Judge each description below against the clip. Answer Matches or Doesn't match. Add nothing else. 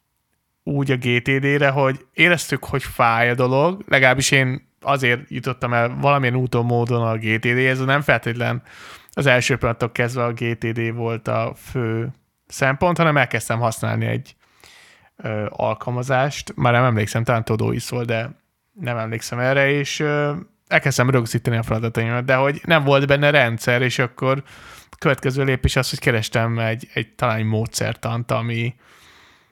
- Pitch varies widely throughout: Doesn't match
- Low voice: Matches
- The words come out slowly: Doesn't match